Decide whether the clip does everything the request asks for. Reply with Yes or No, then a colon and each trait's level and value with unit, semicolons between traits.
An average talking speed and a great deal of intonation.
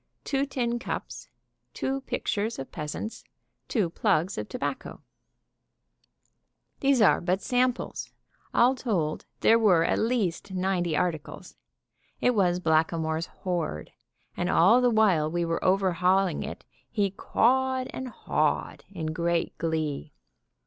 No: slow, 120 wpm; wide, 5.8 semitones